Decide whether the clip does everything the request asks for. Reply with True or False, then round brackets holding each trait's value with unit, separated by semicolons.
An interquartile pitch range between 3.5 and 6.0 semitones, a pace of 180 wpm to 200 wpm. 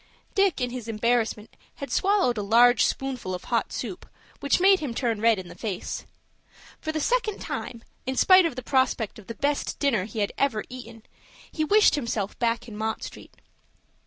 True (4.5 semitones; 190 wpm)